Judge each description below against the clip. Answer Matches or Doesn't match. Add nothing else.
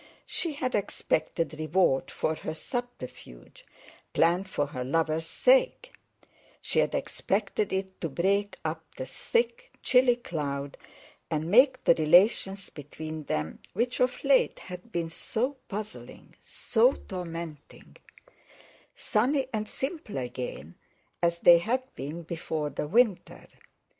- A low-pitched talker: Doesn't match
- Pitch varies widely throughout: Matches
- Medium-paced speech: Doesn't match